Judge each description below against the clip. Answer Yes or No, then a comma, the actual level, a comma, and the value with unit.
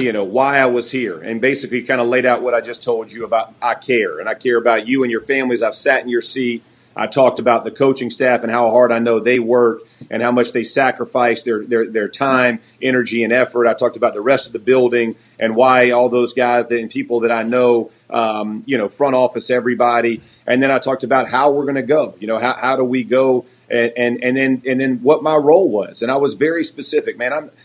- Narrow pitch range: Yes, narrow, 1.7 semitones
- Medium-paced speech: No, fast, 250 wpm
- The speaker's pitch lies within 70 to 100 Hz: No, low, 125 Hz